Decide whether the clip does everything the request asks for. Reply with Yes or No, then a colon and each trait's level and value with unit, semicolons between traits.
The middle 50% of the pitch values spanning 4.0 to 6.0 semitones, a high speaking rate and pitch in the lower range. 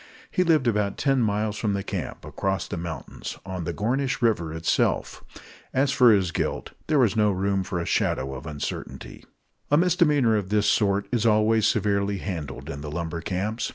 No: average, 4.5 semitones; average, 185 wpm; low, 105 Hz